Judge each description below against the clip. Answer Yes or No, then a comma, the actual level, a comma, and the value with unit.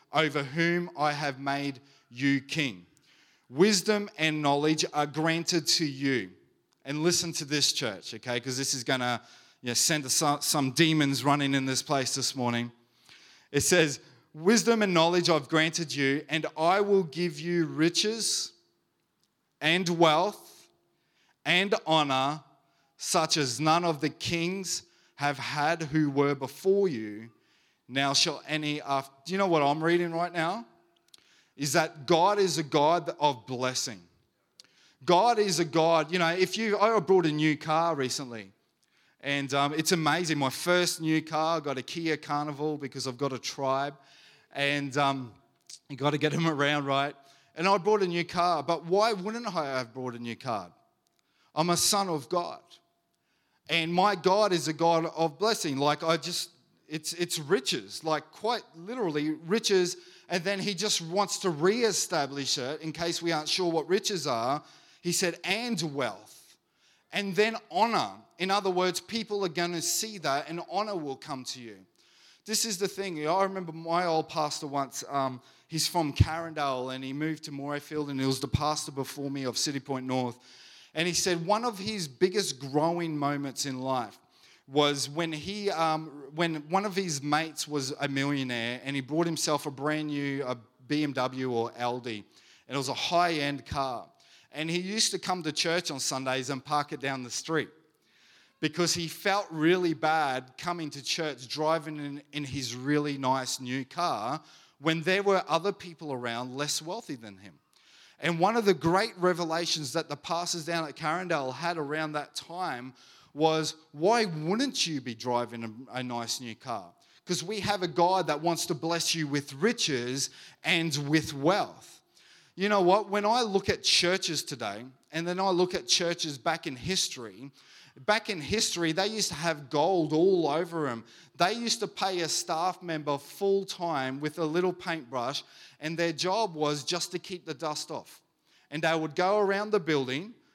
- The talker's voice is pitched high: No, medium, 155 Hz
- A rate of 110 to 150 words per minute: No, average, 180 wpm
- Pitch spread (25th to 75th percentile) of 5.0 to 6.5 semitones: No, average, 4.0 semitones